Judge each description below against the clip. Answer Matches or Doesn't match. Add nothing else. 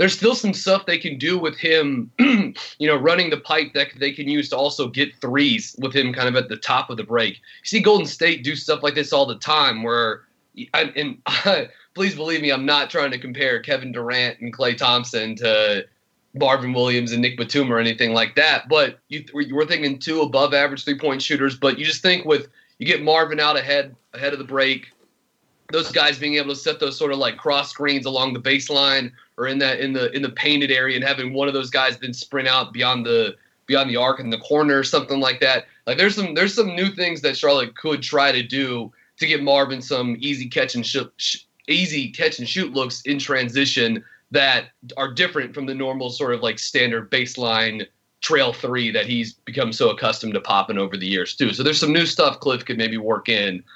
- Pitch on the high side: Doesn't match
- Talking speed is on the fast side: Matches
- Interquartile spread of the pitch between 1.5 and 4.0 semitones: Matches